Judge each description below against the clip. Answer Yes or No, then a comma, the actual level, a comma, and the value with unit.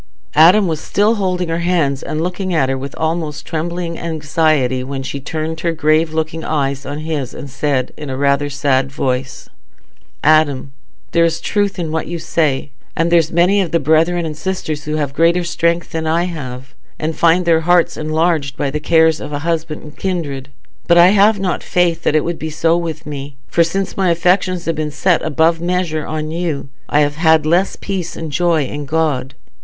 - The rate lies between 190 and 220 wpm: Yes, average, 195 wpm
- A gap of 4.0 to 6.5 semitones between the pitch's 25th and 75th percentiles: No, average, 2.7 semitones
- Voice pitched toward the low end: No, medium, 160 Hz